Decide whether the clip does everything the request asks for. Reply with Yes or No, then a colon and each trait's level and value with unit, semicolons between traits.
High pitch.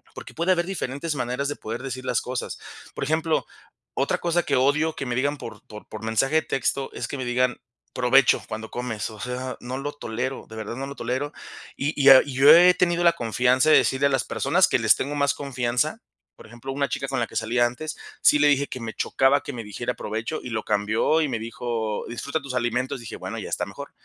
No: low, 130 Hz